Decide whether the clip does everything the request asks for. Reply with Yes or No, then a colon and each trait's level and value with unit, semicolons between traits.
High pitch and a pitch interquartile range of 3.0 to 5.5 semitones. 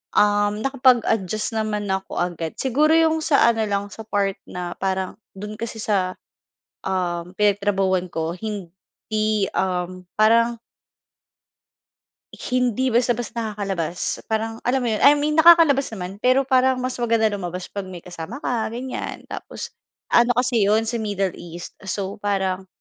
Yes: high, 210 Hz; average, 4.2 semitones